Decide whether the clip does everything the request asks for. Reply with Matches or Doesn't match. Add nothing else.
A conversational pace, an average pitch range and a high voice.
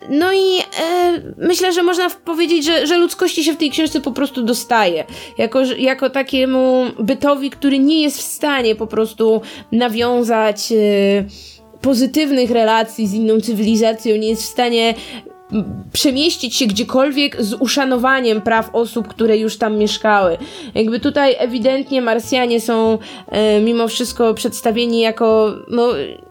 Matches